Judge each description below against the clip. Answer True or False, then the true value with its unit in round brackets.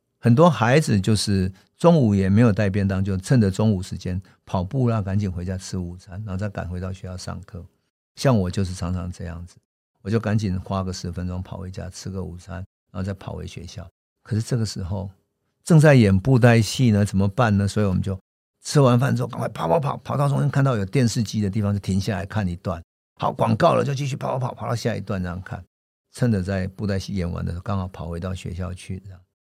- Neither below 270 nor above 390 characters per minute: True (335 characters per minute)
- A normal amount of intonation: True (3.6 semitones)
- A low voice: True (100 Hz)